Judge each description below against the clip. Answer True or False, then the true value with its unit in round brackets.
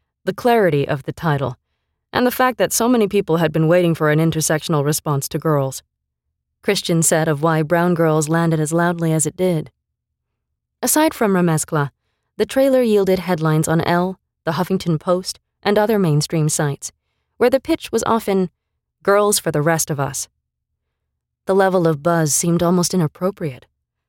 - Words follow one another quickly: False (165 wpm)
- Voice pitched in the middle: True (165 Hz)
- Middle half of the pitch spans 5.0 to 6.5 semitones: False (3.9 semitones)